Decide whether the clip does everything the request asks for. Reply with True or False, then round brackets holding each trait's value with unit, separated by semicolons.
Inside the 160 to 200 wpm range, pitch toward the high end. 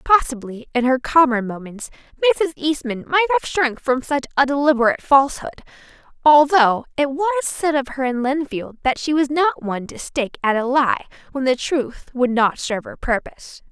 True (180 wpm; 270 Hz)